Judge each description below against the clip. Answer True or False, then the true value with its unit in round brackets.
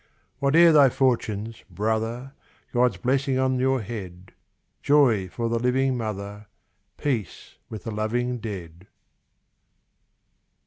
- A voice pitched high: False (115 Hz)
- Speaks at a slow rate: True (105 wpm)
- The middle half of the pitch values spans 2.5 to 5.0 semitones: True (3.9 semitones)